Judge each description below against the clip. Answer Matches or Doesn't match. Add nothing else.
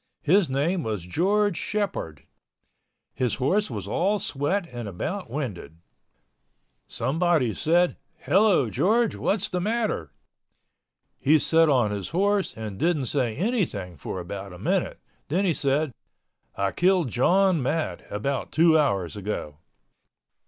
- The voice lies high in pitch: Doesn't match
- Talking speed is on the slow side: Matches